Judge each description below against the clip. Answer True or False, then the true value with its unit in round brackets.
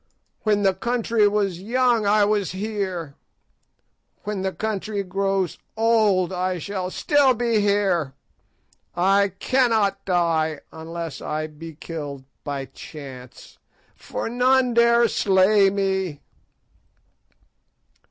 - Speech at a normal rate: False (105 wpm)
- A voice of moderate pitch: False (195 Hz)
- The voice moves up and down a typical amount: True (4.0 semitones)